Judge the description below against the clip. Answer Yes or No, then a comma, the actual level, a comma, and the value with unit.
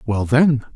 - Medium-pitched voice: No, low, 125 Hz